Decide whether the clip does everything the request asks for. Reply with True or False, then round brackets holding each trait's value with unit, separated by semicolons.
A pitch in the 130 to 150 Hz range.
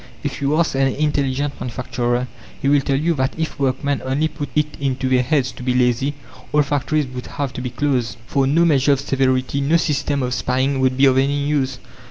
True (135 Hz)